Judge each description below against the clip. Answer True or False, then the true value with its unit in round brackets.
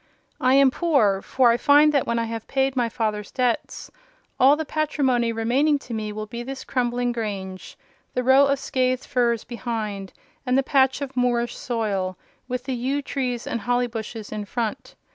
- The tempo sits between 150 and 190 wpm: True (180 wpm)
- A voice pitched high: True (245 Hz)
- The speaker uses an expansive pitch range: False (2.9 semitones)